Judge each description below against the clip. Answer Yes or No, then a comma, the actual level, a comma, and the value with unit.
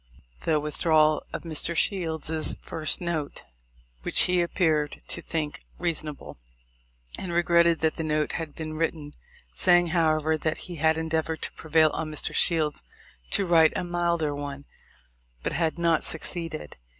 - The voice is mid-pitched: Yes, medium, 160 Hz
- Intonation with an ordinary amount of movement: No, narrow, 1.6 semitones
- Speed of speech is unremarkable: Yes, average, 150 wpm